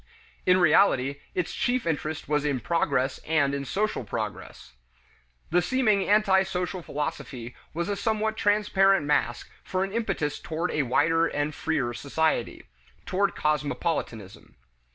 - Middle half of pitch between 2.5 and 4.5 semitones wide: No, average, 5.2 semitones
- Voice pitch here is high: No, medium, 165 Hz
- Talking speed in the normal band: No, slow, 130 wpm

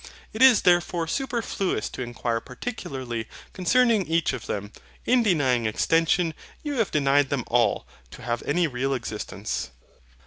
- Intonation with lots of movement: Yes, wide, 8.1 semitones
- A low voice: No, medium, 145 Hz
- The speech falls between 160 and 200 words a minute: No, average, 140 wpm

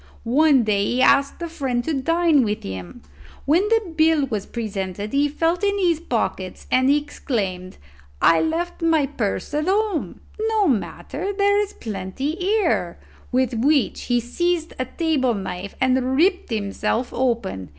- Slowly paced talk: No, average, 150 wpm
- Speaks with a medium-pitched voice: No, very high, 275 Hz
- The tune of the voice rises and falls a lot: Yes, wide, 7.0 semitones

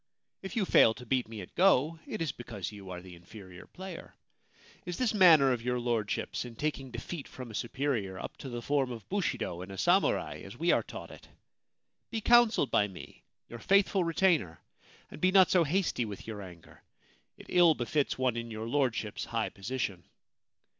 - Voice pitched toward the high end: No, low, 125 Hz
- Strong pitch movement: Yes, wide, 7.9 semitones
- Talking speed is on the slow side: No, average, 195 wpm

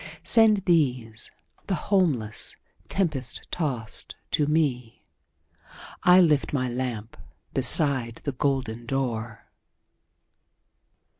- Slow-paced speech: Yes, slow, 80 wpm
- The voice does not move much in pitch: No, average, 4.9 semitones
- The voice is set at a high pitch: No, low, 135 Hz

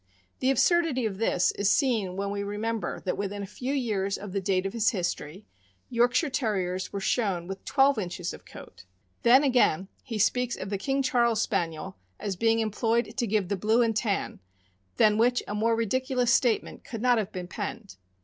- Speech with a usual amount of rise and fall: Yes, average, 3.9 semitones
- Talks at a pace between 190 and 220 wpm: Yes, average, 195 wpm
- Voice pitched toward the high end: Yes, high, 220 Hz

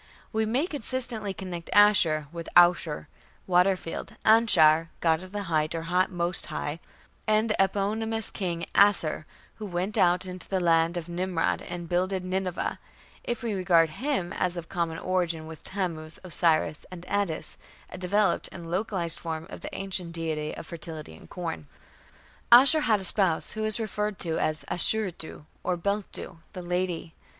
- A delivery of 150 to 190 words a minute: Yes, average, 160 wpm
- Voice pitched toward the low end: No, medium, 180 Hz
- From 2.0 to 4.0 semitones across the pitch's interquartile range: Yes, average, 3.5 semitones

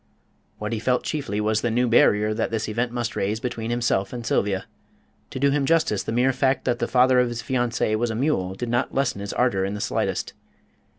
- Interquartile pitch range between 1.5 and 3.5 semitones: Yes, average, 2.8 semitones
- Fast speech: Yes, fast, 225 wpm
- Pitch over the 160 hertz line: No, low, 120 Hz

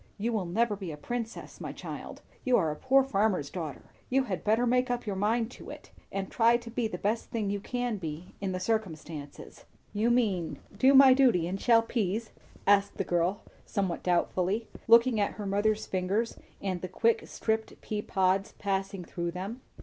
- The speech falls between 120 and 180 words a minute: No, average, 190 wpm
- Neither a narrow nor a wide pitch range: Yes, average, 3.8 semitones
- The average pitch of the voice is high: Yes, high, 210 Hz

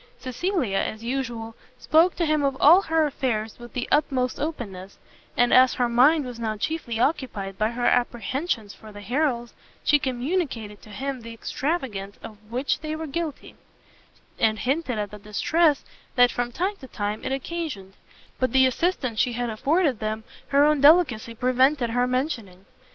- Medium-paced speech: Yes, average, 165 wpm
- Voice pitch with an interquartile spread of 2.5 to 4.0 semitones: No, average, 4.8 semitones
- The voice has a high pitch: Yes, very high, 250 Hz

